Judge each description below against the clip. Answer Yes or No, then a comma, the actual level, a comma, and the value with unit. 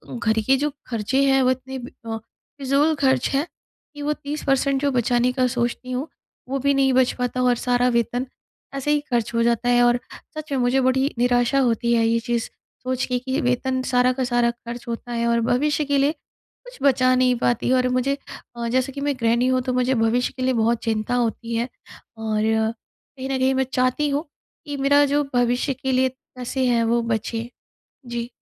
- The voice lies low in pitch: No, very high, 250 Hz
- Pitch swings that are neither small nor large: No, narrow, 2.1 semitones